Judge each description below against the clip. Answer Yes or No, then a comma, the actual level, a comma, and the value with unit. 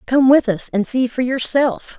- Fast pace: Yes, fast, 210 wpm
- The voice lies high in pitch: Yes, very high, 250 Hz